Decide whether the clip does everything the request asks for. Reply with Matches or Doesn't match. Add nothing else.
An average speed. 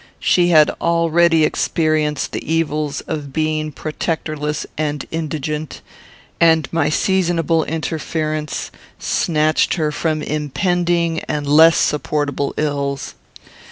Doesn't match